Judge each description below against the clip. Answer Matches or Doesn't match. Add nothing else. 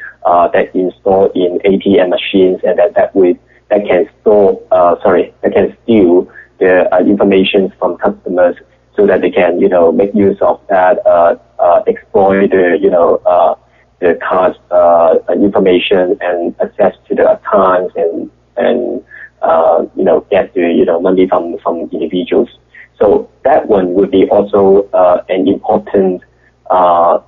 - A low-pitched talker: Matches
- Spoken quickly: Doesn't match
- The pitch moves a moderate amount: Doesn't match